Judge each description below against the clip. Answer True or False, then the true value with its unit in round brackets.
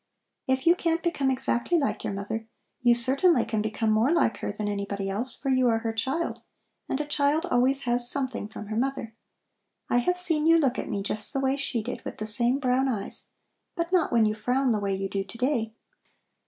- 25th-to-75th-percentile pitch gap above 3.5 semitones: True (4.1 semitones)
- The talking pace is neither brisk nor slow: False (220 wpm)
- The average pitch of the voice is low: False (245 Hz)